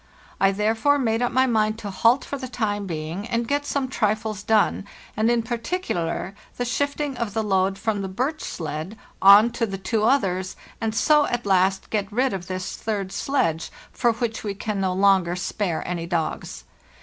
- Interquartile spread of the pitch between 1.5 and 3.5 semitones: No, average, 3.9 semitones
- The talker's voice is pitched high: Yes, high, 215 Hz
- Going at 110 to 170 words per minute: No, average, 185 wpm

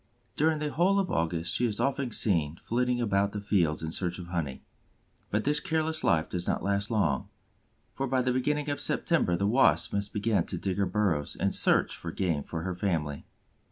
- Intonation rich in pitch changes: Yes, wide, 6.7 semitones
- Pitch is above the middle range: No, low, 100 Hz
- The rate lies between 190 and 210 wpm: Yes, average, 200 wpm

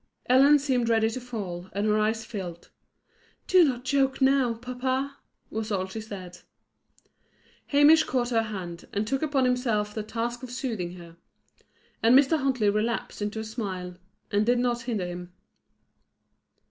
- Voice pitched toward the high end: Yes, high, 230 Hz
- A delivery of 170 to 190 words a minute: No, average, 155 wpm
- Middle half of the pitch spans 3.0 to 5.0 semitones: Yes, average, 3.9 semitones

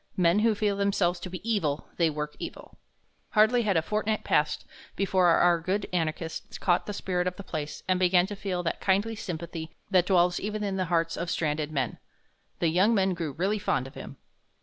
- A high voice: No, medium, 180 Hz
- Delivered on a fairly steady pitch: No, average, 3.4 semitones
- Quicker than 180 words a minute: Yes, average, 200 wpm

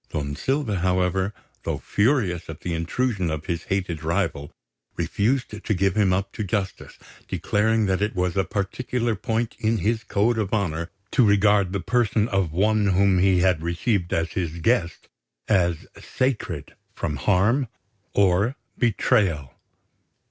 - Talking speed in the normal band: Yes, average, 150 wpm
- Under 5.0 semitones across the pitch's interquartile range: Yes, average, 3.7 semitones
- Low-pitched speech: Yes, low, 100 Hz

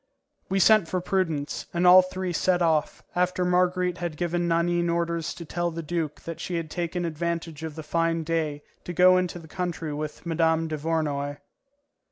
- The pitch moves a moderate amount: No, narrow, 1.8 semitones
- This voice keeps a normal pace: Yes, average, 180 wpm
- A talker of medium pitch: Yes, medium, 170 Hz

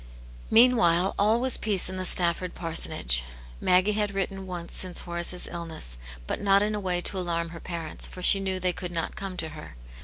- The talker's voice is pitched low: No, medium, 180 Hz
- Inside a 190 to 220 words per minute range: Yes, average, 195 wpm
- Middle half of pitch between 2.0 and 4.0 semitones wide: Yes, narrow, 2.5 semitones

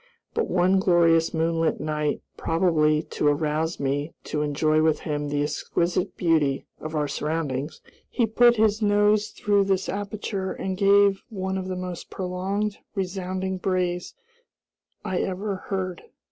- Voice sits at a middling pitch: Yes, medium, 180 Hz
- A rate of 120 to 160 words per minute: Yes, average, 140 wpm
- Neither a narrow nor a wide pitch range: Yes, average, 3.9 semitones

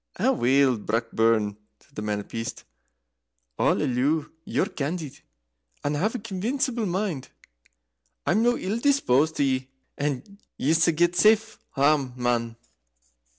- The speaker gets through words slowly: Yes, slow, 125 wpm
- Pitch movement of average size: No, wide, 7.8 semitones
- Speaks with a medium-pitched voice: Yes, medium, 145 Hz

